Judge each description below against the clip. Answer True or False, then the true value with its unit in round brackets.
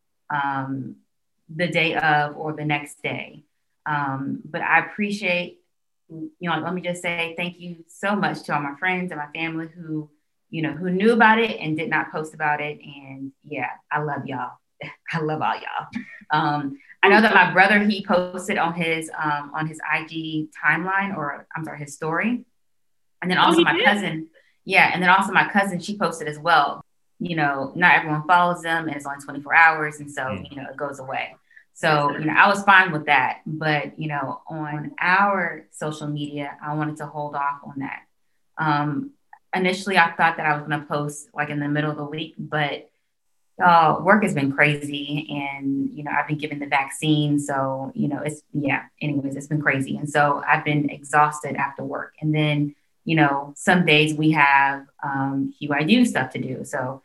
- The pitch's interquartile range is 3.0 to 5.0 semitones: False (2.6 semitones)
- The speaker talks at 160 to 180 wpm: False (195 wpm)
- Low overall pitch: False (150 Hz)